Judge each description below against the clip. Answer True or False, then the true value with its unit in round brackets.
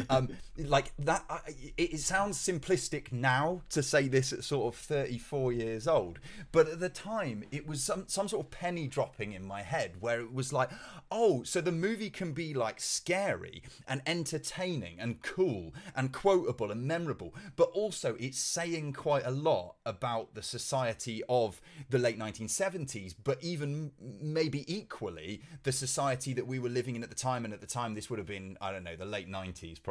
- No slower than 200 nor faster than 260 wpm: False (190 wpm)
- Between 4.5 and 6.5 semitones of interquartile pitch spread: True (5.6 semitones)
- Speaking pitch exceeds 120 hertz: True (140 Hz)